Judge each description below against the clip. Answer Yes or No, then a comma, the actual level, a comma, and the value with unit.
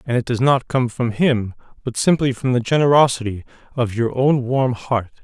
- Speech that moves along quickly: No, average, 195 wpm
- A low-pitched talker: Yes, low, 125 Hz